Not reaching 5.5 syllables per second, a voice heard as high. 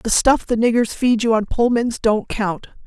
Yes: 4.5 syllables/s; high, 225 Hz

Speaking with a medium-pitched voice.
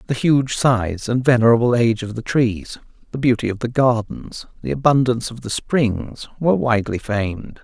No: low, 120 Hz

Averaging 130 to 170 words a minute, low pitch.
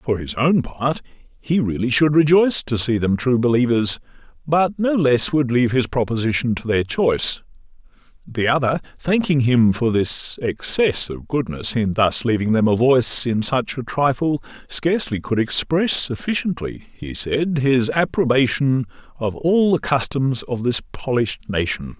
Yes: average, 160 wpm; low, 130 Hz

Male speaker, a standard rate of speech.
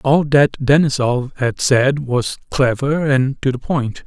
Yes: male; average, 160 wpm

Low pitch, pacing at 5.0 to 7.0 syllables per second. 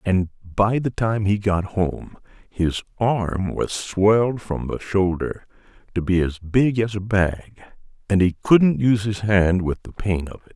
No: low, 100 Hz; 4.2 syllables/s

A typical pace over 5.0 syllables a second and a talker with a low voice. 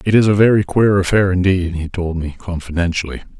Yes: 5.9 syllables/s; very low, 90 Hz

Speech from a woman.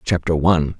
No: male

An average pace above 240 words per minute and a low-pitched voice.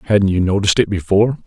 No: fast, 205 wpm; low, 100 Hz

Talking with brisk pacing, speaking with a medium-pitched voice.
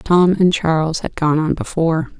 No: average, 190 wpm; medium, 165 Hz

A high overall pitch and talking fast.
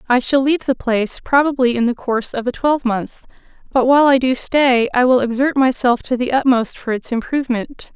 Yes: very high, 255 Hz; fast, 210 wpm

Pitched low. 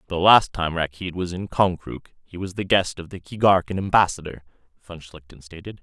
Yes: very low, 90 Hz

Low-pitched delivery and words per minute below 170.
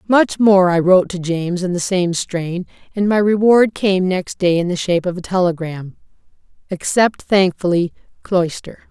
No: medium, 185 Hz; average, 160 wpm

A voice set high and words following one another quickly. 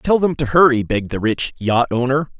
No: low, 130 Hz; fast, 225 wpm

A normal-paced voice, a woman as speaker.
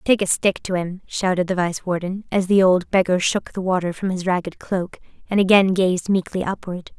No: fast, 215 wpm; female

